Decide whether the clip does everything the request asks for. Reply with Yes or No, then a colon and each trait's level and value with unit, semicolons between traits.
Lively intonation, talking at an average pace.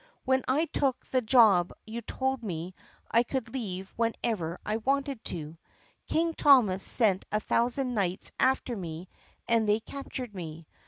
Yes: wide, 5.8 semitones; average, 150 wpm